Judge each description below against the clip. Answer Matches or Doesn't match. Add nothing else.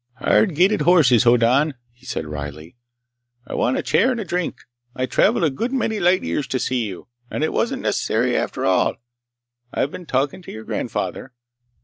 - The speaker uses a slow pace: Doesn't match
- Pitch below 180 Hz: Matches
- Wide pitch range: Matches